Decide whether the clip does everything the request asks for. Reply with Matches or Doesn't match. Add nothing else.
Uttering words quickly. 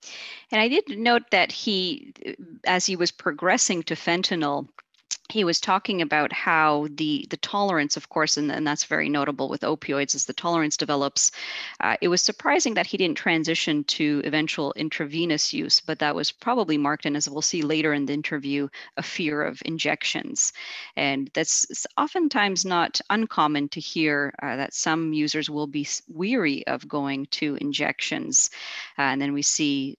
Doesn't match